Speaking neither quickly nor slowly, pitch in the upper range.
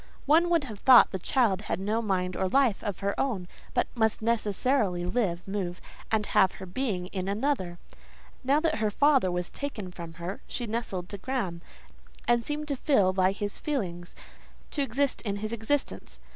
Yes: average, 180 wpm; high, 210 Hz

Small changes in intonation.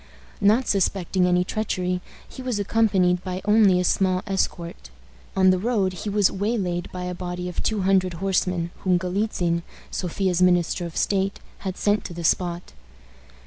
Yes: narrow, 1.8 semitones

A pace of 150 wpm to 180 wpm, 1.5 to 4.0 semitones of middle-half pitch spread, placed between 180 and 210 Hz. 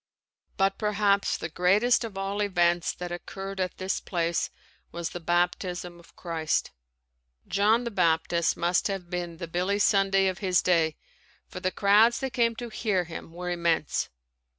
Yes: average, 160 wpm; narrow, 2.6 semitones; medium, 185 Hz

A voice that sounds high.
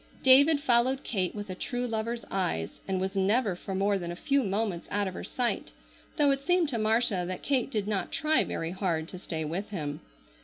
Yes: high, 205 Hz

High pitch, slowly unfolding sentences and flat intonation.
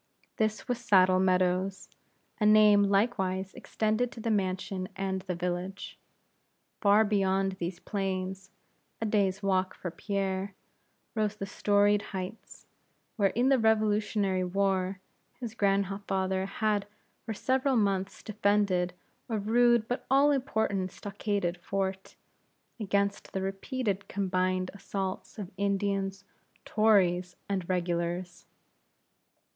Yes: high, 195 Hz; slow, 115 wpm; narrow, 2.1 semitones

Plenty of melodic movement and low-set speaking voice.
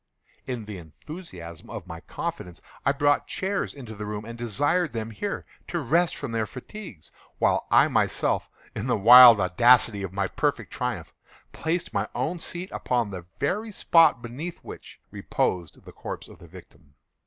Yes: wide, 8.3 semitones; low, 120 Hz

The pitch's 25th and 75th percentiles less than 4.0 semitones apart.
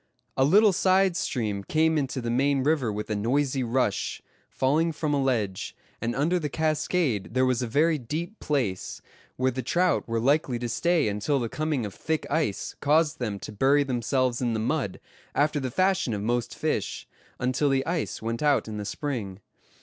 No: average, 4.9 semitones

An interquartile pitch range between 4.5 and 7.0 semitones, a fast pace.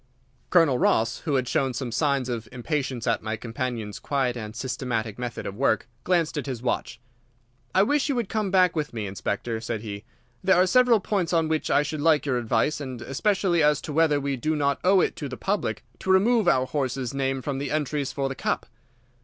Yes: average, 5.1 semitones; fast, 210 wpm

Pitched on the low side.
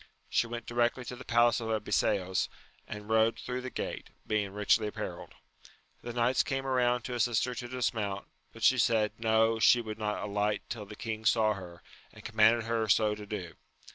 Yes: low, 110 Hz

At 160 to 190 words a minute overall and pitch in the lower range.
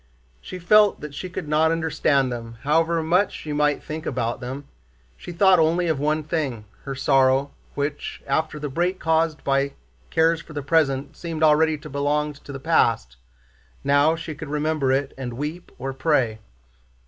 No: average, 170 wpm; medium, 150 Hz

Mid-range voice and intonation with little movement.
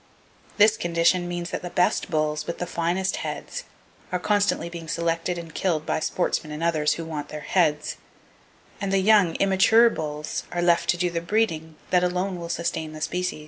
Yes: medium, 170 Hz; narrow, 2.3 semitones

